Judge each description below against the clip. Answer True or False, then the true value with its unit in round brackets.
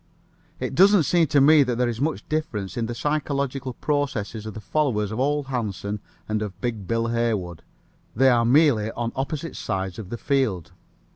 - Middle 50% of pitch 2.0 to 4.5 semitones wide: False (5.0 semitones)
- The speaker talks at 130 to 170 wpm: False (185 wpm)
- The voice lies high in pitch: False (120 Hz)